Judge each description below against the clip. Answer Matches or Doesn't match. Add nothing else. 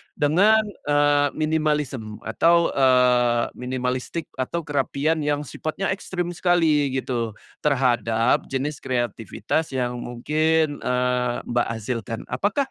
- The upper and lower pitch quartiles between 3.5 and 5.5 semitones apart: Matches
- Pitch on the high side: Doesn't match